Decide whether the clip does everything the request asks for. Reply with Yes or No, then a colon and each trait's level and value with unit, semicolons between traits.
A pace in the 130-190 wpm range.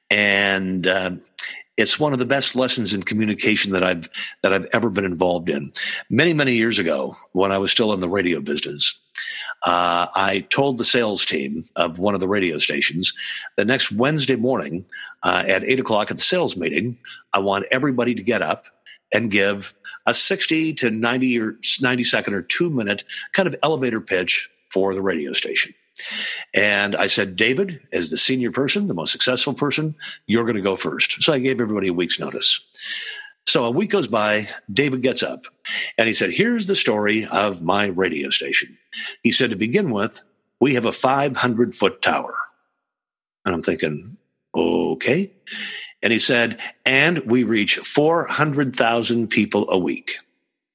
Yes: average, 175 wpm